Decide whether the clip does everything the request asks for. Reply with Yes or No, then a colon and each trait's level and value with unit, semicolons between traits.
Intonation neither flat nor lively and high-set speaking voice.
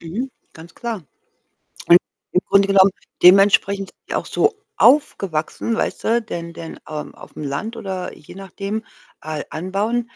Yes: average, 4.7 semitones; high, 195 Hz